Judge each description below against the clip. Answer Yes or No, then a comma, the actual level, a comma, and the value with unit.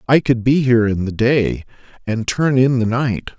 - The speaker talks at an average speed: No, fast, 215 wpm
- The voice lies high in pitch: No, low, 120 Hz